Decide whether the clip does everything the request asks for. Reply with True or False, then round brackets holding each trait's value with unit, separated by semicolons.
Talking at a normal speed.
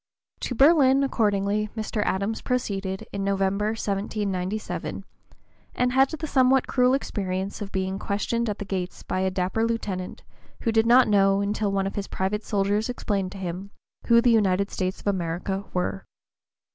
True (160 wpm)